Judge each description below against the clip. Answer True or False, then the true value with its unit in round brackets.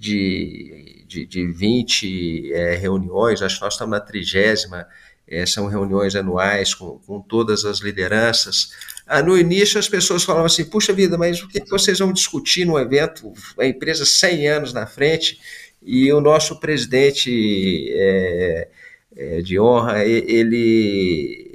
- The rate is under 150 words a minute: False (155 wpm)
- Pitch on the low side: True (120 Hz)